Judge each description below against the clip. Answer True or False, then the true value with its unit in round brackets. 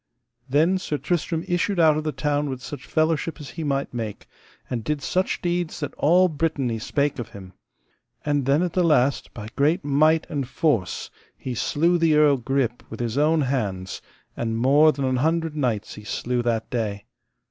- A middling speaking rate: True (185 wpm)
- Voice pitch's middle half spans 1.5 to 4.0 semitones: False (4.4 semitones)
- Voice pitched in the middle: True (145 Hz)